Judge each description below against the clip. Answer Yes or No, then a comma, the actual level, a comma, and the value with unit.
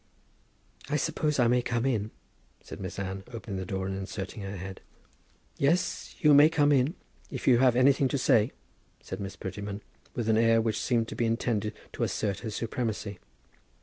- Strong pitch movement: No, average, 4.4 semitones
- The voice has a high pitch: No, low, 115 Hz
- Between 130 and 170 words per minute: No, average, 180 wpm